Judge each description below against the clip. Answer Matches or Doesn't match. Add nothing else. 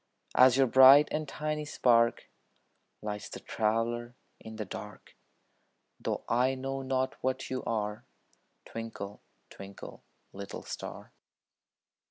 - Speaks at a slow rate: Matches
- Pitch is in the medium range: Doesn't match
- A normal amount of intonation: Matches